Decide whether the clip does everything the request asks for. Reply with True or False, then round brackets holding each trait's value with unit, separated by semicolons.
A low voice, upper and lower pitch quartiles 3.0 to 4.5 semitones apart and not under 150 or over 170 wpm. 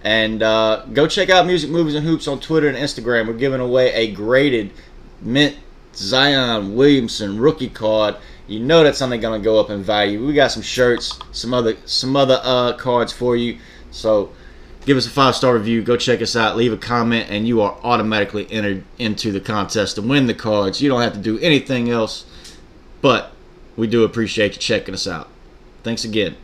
False (115 Hz; 3.3 semitones; 200 wpm)